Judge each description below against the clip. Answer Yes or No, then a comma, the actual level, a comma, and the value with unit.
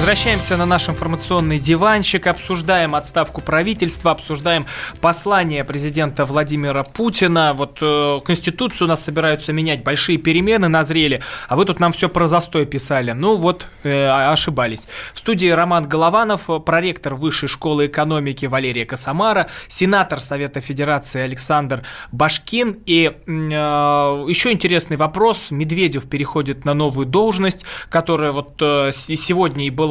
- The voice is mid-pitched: Yes, medium, 155 Hz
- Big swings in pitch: No, average, 3.5 semitones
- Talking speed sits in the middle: Yes, average, 130 wpm